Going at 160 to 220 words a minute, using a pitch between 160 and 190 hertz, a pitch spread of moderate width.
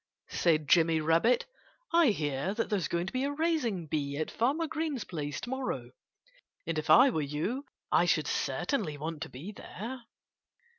No: average, 170 wpm; medium, 185 Hz; wide, 8.9 semitones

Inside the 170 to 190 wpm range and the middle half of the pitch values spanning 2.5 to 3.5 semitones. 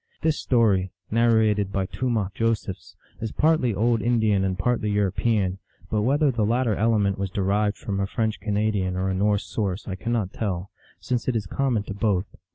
Yes: average, 180 wpm; average, 3.0 semitones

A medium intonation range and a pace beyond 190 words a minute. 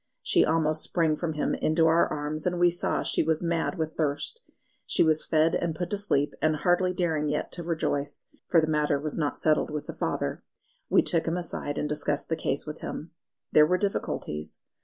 No: narrow, 2.1 semitones; fast, 205 wpm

